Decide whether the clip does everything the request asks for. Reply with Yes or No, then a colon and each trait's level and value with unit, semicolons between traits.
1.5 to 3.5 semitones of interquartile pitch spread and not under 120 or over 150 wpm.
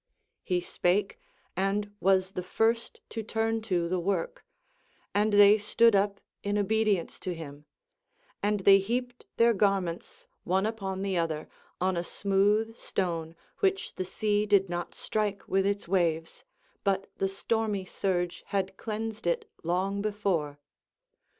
Yes: average, 2.7 semitones; average, 140 wpm